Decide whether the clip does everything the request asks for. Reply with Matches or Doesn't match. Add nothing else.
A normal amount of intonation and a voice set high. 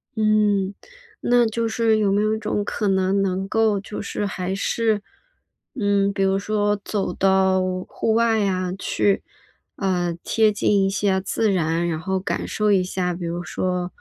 Doesn't match